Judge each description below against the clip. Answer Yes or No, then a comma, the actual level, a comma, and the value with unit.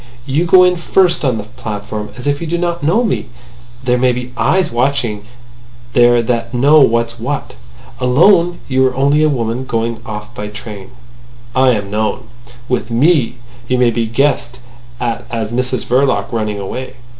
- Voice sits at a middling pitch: No, low, 125 Hz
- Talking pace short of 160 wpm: No, average, 170 wpm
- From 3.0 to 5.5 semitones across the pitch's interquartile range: Yes, average, 3.6 semitones